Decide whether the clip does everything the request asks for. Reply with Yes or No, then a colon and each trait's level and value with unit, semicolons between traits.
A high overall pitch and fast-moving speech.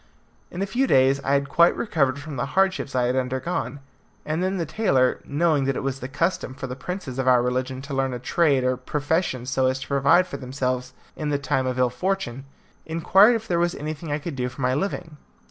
No: medium, 140 Hz; fast, 225 wpm